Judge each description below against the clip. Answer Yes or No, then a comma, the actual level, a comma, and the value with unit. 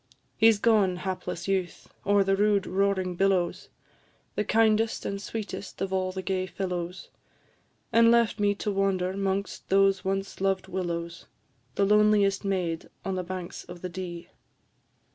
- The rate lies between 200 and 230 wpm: No, average, 150 wpm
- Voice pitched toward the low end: No, high, 195 Hz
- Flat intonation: Yes, narrow, 1.7 semitones